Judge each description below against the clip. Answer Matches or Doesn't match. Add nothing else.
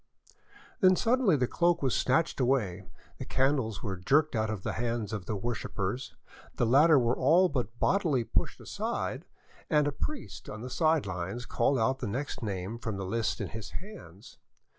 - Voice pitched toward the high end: Doesn't match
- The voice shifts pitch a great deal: Matches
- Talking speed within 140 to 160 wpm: Doesn't match